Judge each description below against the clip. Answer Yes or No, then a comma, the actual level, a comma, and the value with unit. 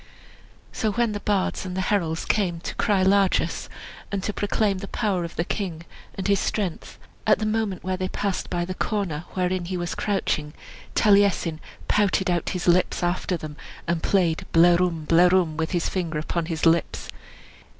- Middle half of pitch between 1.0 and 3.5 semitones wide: Yes, average, 2.8 semitones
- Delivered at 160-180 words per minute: Yes, average, 175 wpm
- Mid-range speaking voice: Yes, medium, 180 Hz